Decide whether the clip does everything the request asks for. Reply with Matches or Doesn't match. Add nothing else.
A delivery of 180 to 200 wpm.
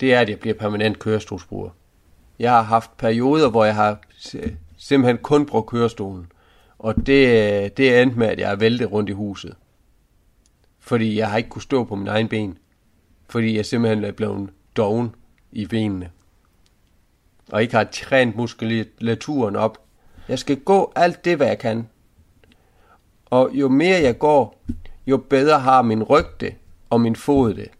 Doesn't match